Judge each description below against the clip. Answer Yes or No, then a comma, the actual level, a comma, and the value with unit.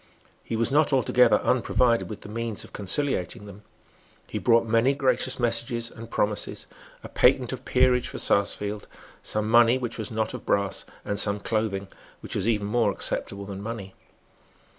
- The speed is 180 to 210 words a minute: No, average, 165 wpm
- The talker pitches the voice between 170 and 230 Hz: No, low, 115 Hz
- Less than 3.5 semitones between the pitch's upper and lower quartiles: Yes, narrow, 2.6 semitones